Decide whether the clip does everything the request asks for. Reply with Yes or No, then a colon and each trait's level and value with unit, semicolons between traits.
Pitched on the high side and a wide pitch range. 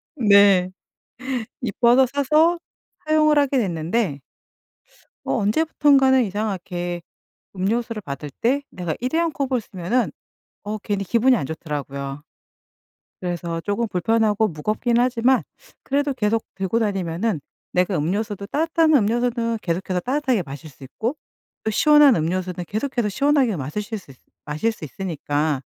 Yes: high, 210 Hz; wide, 6.2 semitones